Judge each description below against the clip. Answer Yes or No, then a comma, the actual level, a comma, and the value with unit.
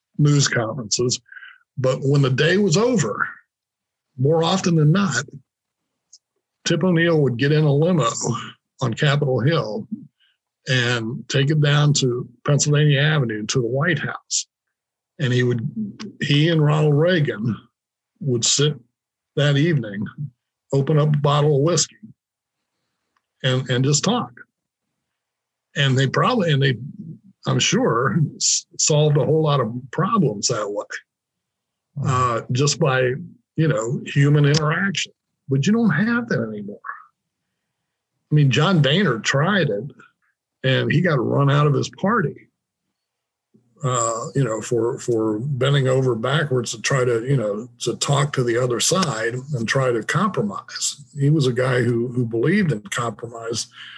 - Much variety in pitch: No, average, 3.8 semitones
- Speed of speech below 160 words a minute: Yes, average, 140 wpm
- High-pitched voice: No, medium, 140 Hz